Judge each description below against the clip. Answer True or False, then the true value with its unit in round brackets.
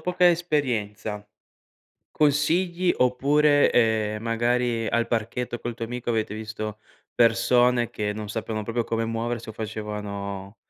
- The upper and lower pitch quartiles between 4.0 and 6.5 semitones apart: False (2.5 semitones)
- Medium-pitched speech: False (115 Hz)